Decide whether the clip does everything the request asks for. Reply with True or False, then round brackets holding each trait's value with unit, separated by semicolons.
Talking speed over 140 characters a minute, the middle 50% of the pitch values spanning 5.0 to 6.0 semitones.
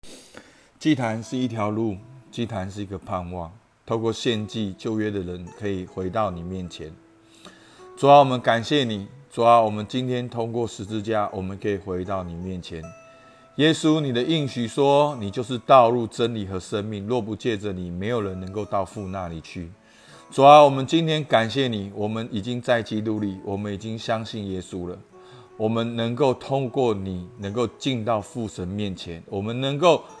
False (260 characters per minute; 4.1 semitones)